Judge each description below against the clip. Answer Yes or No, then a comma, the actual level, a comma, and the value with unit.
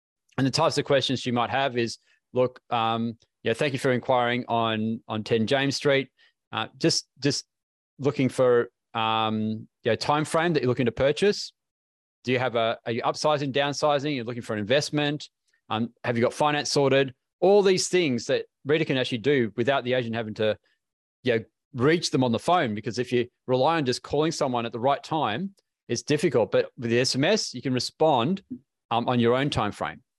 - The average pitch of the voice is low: Yes, low, 130 Hz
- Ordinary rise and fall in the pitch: Yes, average, 4.1 semitones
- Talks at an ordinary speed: Yes, average, 195 wpm